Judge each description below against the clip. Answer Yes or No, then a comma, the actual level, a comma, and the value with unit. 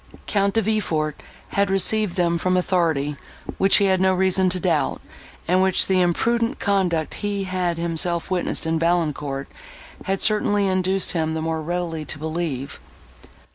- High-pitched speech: No, medium, 180 Hz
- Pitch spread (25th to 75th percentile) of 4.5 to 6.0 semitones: No, average, 3.0 semitones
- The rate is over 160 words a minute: No, average, 155 wpm